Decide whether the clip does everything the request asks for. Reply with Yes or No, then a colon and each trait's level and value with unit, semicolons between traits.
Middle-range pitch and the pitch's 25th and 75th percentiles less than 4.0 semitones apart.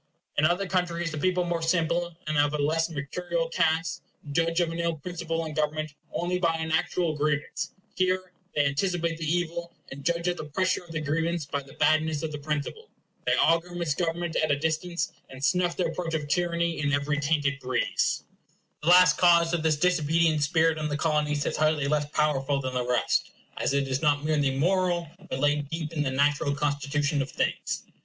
Yes: medium, 160 Hz; average, 2.7 semitones